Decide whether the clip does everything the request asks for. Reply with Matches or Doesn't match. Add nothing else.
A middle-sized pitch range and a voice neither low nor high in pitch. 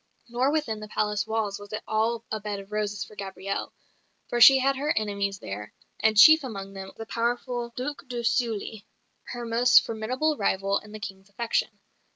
Doesn't match